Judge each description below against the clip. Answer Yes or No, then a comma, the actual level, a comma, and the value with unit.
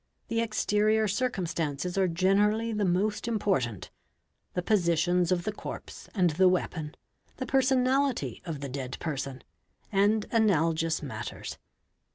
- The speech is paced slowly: Yes, slow, 120 wpm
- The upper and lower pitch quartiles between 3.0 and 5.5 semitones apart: Yes, average, 4.9 semitones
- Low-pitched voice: No, medium, 185 Hz